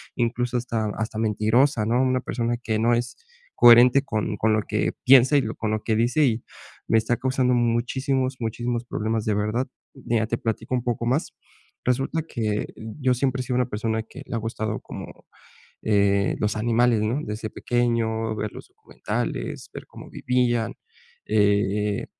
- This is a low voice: Yes, low, 115 Hz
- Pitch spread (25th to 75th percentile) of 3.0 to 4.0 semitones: No, narrow, 2.4 semitones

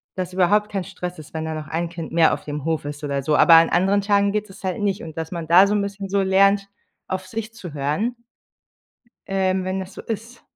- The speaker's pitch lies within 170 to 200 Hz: Yes, medium, 185 Hz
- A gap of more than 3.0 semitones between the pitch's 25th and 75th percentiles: Yes, average, 3.7 semitones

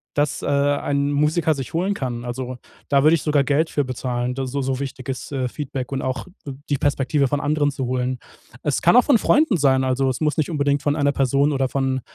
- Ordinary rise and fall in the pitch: No, narrow, 2.1 semitones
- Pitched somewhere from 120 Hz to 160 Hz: Yes, medium, 140 Hz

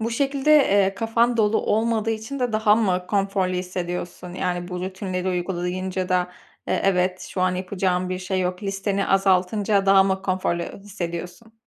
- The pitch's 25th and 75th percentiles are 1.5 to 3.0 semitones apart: Yes, narrow, 2.6 semitones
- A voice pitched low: No, high, 190 Hz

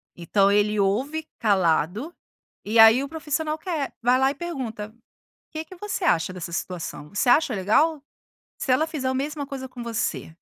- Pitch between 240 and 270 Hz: Yes, very high, 255 Hz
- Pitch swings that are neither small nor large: No, wide, 6.9 semitones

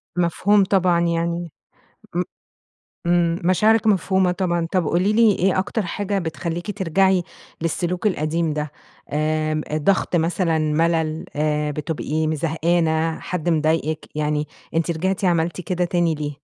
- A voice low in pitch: No, medium, 170 Hz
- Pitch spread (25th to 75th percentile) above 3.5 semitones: No, average, 2.7 semitones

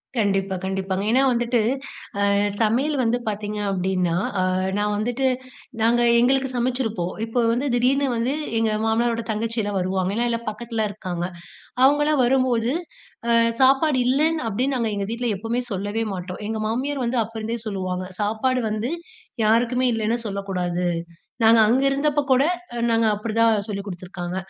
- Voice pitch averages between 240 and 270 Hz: No, high, 225 Hz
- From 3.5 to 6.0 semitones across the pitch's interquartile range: Yes, average, 3.8 semitones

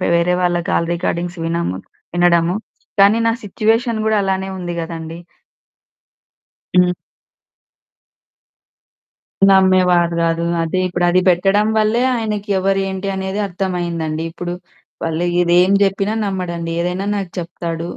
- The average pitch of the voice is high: No, medium, 180 Hz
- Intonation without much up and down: Yes, narrow, 2.3 semitones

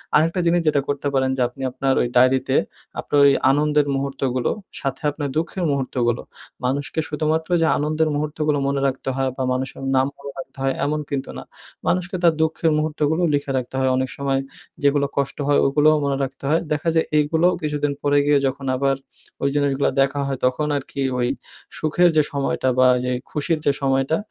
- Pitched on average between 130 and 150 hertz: Yes, medium, 140 Hz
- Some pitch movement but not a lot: No, narrow, 2.2 semitones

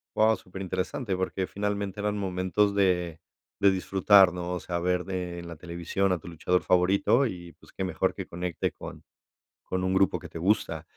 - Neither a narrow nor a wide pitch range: No, narrow, 1.8 semitones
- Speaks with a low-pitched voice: Yes, very low, 95 Hz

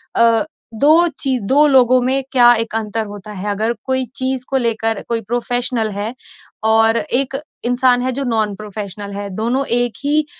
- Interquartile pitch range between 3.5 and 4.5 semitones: No, average, 3.0 semitones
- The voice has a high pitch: Yes, high, 235 Hz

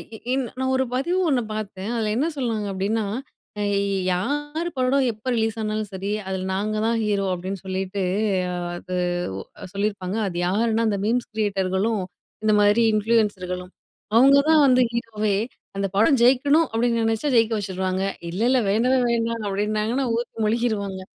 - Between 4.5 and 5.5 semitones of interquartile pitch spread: No, average, 3.5 semitones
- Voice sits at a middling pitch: No, high, 215 Hz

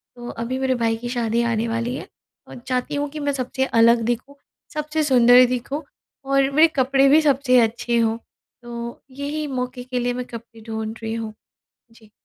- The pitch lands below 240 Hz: No, high, 245 Hz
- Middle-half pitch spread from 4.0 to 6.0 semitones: No, average, 2.7 semitones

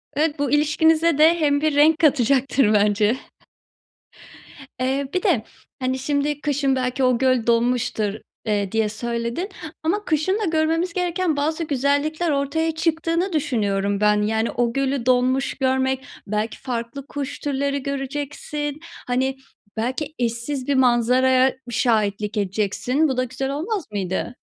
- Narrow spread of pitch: No, average, 4.2 semitones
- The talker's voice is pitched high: Yes, very high, 270 Hz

